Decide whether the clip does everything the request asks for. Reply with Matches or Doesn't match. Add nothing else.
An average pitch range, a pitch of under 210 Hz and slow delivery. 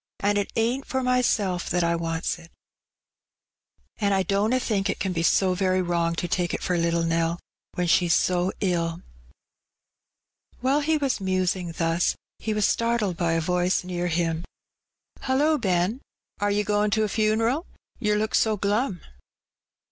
Doesn't match